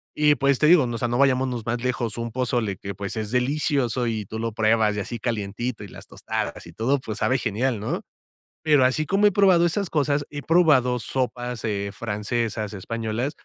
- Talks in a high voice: No, low, 120 Hz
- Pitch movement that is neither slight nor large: Yes, average, 4.0 semitones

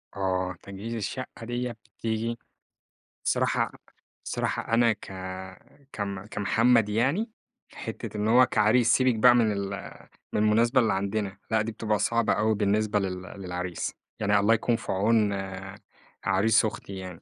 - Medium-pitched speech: No, low, 110 Hz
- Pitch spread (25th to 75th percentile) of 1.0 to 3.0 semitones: Yes, average, 2.7 semitones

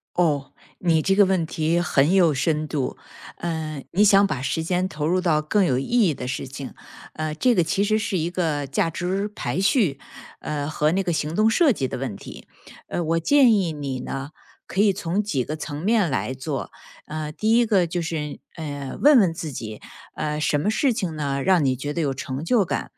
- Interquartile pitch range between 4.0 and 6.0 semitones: Yes, average, 4.9 semitones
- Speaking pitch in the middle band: Yes, medium, 165 Hz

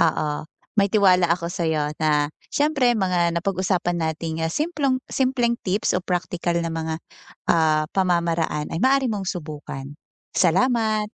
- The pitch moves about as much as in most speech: Yes, average, 4.7 semitones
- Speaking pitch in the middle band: Yes, medium, 175 Hz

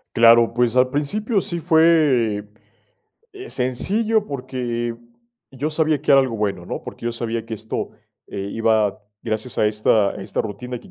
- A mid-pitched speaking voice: No, low, 120 Hz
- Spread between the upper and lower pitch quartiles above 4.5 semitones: Yes, average, 5.3 semitones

